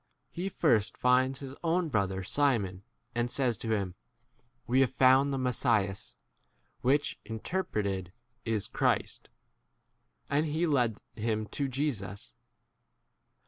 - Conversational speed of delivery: No, slow, 130 wpm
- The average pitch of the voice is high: No, low, 125 Hz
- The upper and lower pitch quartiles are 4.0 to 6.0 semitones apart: Yes, average, 5.0 semitones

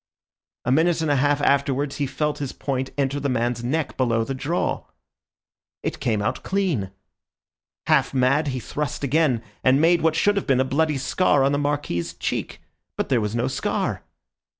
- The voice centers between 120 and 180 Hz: Yes, medium, 140 Hz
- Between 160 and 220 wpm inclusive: Yes, average, 180 wpm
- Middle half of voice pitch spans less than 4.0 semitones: Yes, average, 2.9 semitones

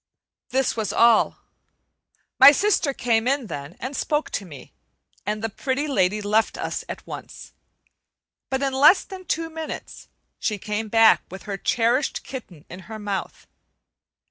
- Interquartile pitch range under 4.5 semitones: No, average, 5.1 semitones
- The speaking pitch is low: No, high, 230 Hz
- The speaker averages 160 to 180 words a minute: No, average, 150 wpm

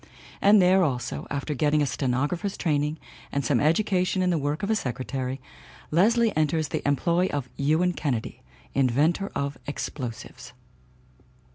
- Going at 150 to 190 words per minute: No, average, 140 wpm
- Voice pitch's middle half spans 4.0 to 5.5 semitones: Yes, average, 4.8 semitones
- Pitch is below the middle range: No, medium, 150 Hz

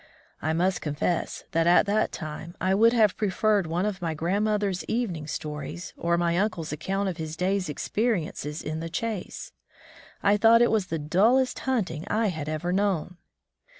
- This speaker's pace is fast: No, average, 165 wpm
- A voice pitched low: No, medium, 185 Hz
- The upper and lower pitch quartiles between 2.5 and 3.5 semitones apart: No, average, 4.4 semitones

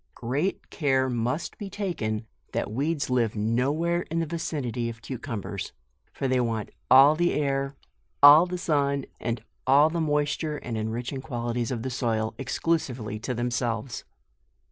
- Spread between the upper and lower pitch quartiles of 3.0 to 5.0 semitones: Yes, average, 4.3 semitones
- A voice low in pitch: Yes, low, 130 Hz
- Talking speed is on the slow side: No, average, 160 wpm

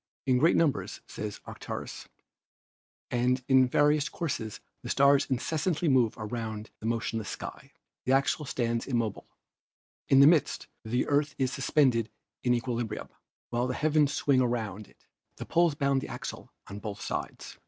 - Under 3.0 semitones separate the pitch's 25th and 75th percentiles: No, average, 3.6 semitones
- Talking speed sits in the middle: Yes, average, 155 wpm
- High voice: No, low, 130 Hz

